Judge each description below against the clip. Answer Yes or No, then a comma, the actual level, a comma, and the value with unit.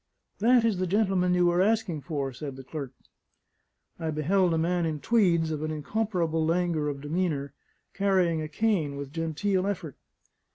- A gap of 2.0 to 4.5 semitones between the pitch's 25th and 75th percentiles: Yes, average, 3.9 semitones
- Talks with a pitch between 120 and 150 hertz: No, medium, 170 Hz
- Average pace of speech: Yes, average, 170 wpm